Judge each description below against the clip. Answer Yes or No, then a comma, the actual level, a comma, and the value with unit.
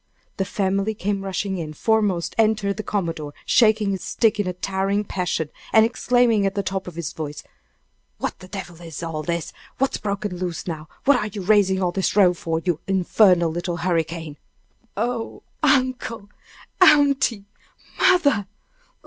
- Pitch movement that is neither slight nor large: Yes, average, 3.8 semitones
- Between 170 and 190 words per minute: No, average, 155 wpm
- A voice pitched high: Yes, high, 195 Hz